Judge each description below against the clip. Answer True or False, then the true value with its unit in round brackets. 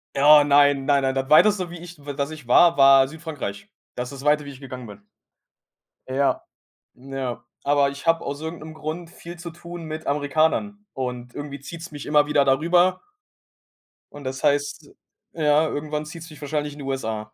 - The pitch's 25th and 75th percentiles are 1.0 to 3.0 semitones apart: True (2.7 semitones)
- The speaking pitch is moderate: True (145 Hz)